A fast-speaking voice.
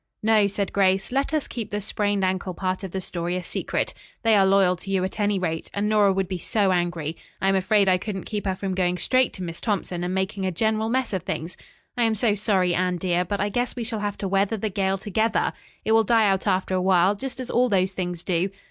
Yes: fast, 255 wpm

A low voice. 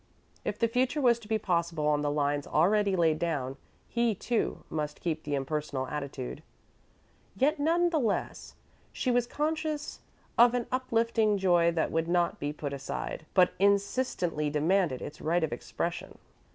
No: medium, 175 Hz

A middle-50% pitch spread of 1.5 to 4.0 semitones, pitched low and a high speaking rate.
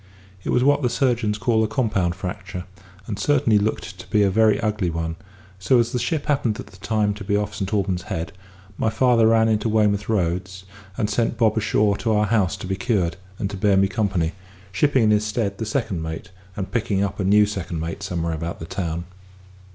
Yes: average, 3.0 semitones; low, 105 Hz; fast, 215 wpm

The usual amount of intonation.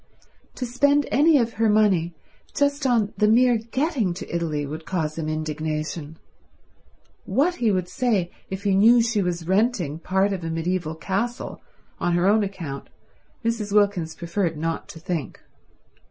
No: wide, 5.7 semitones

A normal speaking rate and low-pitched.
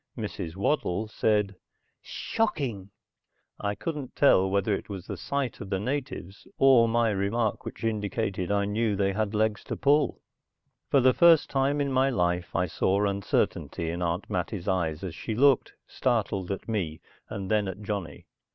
Yes: average, 165 wpm; low, 105 Hz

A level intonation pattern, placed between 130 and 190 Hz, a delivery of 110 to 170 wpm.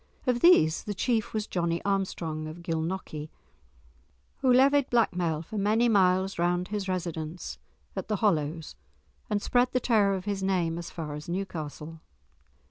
No: average, 4.3 semitones; medium, 185 Hz; average, 150 wpm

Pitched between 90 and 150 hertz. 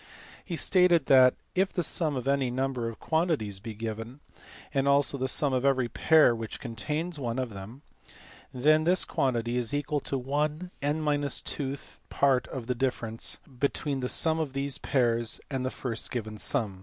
Yes: low, 135 Hz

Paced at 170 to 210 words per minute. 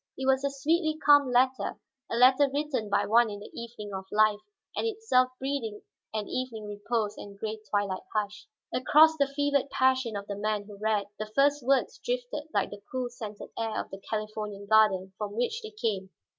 Yes: average, 190 wpm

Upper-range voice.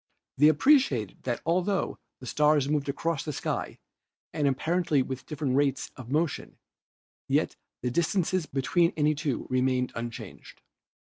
No: medium, 145 Hz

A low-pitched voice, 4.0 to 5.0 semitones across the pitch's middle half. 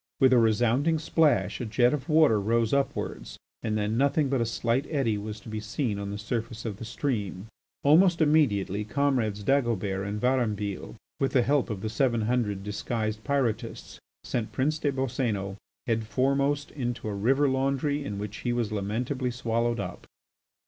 Yes: low, 120 Hz; average, 4.4 semitones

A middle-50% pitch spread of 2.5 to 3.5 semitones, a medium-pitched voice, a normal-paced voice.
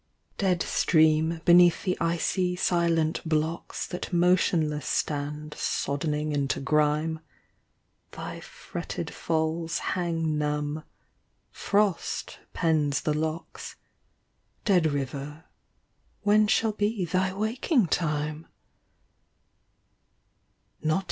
No: average, 2.9 semitones; medium, 160 Hz; slow, 85 wpm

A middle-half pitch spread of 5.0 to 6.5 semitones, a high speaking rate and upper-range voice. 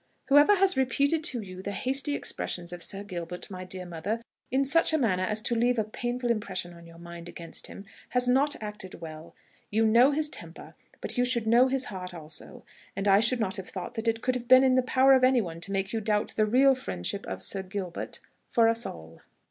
Yes: wide, 5.6 semitones; fast, 225 wpm; high, 220 Hz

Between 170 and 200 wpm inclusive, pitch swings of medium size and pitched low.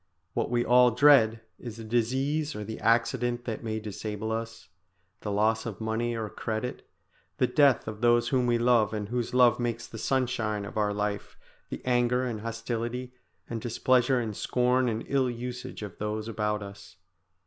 No: average, 175 wpm; narrow, 2.2 semitones; low, 115 Hz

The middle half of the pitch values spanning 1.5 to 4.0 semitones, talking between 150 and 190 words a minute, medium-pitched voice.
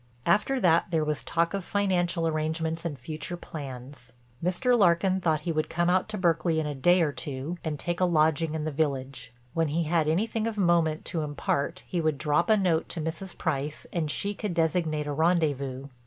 No: narrow, 2.6 semitones; average, 200 wpm; medium, 160 Hz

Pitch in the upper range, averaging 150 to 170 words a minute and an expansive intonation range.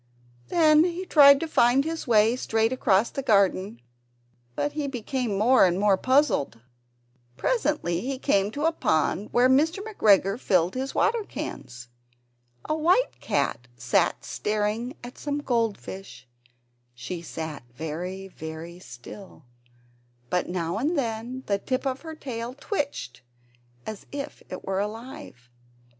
No: high, 225 Hz; slow, 135 wpm; wide, 7.1 semitones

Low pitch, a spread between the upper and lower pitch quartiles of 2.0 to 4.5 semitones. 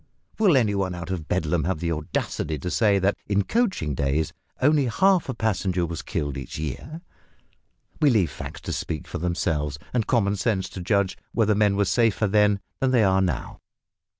No: very low, 95 Hz; average, 5.0 semitones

